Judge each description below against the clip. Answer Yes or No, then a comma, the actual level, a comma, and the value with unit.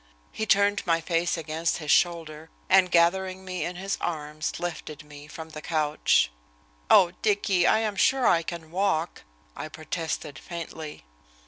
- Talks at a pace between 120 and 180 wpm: Yes, average, 150 wpm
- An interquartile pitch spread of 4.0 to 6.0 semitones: No, average, 3.2 semitones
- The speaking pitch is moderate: Yes, medium, 170 Hz